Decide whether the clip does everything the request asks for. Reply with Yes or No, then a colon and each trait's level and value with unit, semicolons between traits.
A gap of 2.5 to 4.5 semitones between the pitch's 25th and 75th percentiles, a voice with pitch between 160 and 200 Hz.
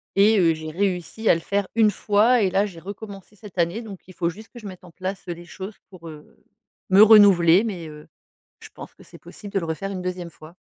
Yes: average, 3.2 semitones; high, 190 Hz